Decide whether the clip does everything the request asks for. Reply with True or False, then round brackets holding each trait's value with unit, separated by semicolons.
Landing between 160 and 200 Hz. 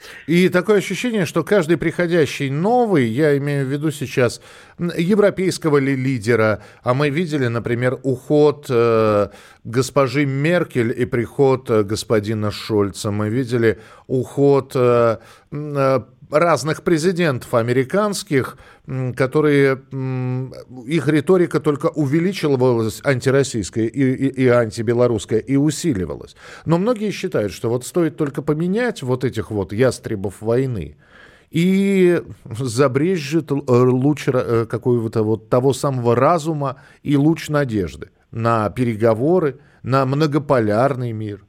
False (135 Hz)